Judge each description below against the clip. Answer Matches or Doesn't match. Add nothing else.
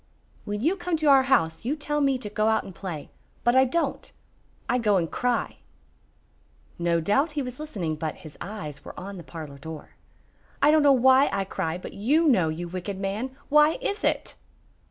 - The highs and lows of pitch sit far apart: Matches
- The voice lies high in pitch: Matches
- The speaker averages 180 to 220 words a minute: Matches